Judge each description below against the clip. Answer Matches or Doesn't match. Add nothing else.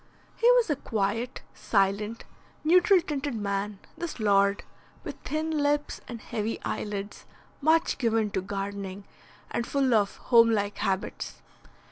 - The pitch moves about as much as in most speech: Doesn't match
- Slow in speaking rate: Matches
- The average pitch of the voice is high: Matches